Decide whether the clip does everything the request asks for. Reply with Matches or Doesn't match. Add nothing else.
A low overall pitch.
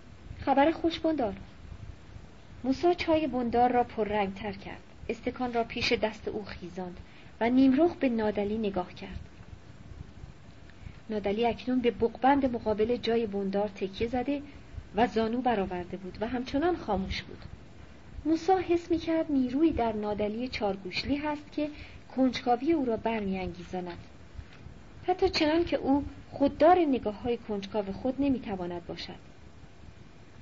Doesn't match